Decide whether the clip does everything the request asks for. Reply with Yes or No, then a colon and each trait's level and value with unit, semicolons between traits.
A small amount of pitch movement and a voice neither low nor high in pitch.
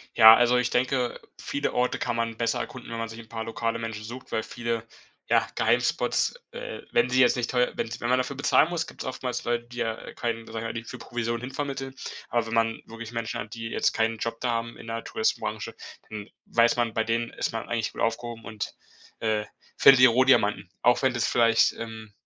No: narrow, 1.5 semitones; low, 115 Hz